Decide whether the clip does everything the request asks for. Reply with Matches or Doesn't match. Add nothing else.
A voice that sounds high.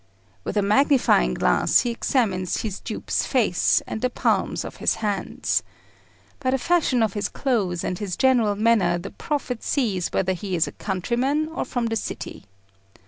Matches